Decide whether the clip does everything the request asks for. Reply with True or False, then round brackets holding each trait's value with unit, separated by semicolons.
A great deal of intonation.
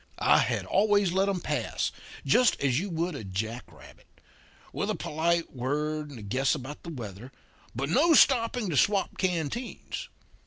True (7.2 semitones)